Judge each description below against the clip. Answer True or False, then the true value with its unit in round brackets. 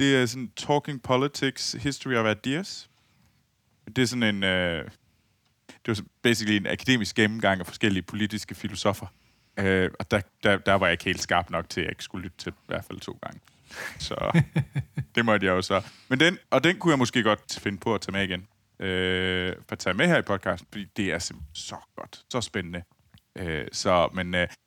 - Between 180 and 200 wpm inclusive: False (210 wpm)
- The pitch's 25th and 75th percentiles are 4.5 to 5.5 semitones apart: True (5.1 semitones)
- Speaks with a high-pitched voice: False (105 Hz)